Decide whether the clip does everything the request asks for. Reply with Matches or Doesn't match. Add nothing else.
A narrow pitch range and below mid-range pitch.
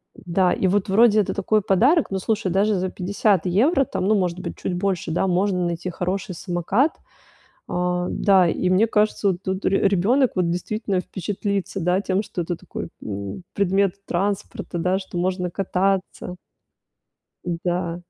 Doesn't match